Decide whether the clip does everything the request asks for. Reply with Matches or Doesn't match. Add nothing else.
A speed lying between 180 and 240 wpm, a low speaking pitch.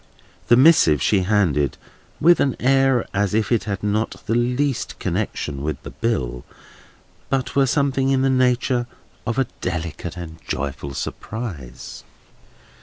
Doesn't match